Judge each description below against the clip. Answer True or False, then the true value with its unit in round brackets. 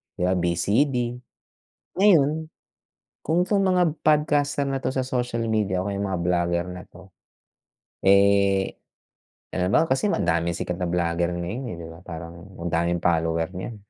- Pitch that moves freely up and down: True (7.7 semitones)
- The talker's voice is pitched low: True (95 Hz)